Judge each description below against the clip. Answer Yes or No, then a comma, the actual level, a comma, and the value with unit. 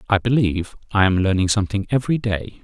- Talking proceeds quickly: No, average, 185 wpm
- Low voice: Yes, low, 105 Hz